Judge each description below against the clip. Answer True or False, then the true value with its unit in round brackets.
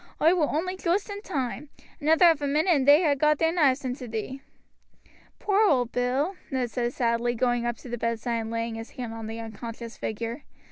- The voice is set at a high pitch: True (255 Hz)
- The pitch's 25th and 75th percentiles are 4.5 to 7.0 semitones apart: True (4.8 semitones)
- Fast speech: True (215 wpm)